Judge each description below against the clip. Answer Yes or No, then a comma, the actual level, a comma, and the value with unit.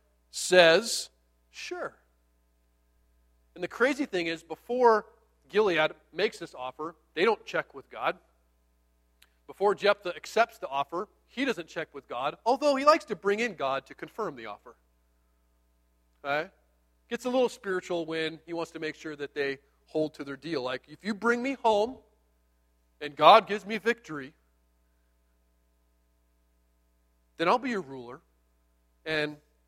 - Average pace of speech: Yes, average, 145 wpm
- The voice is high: No, medium, 140 Hz